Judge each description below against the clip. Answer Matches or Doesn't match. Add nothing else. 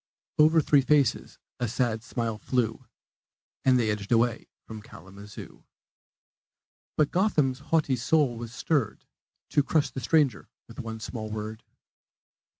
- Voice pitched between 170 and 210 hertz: Doesn't match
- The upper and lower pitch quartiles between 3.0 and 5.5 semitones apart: Matches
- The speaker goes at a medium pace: Doesn't match